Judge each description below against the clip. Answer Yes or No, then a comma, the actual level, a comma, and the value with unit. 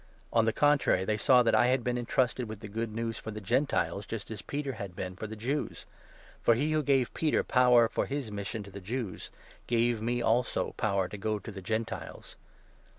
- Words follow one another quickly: Yes, fast, 220 wpm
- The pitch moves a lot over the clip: No, average, 3.0 semitones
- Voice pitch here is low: Yes, low, 115 Hz